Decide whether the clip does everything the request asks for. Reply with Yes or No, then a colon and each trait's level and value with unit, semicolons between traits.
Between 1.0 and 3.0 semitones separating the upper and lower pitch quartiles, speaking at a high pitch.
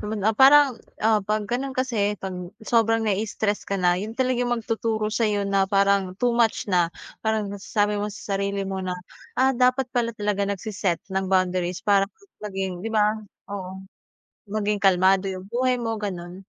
Yes: average, 2.7 semitones; high, 205 Hz